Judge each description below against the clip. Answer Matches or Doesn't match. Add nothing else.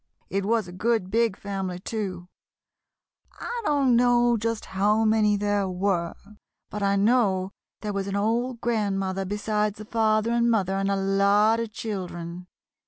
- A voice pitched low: Doesn't match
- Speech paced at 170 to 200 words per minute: Doesn't match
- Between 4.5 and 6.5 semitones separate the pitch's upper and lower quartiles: Doesn't match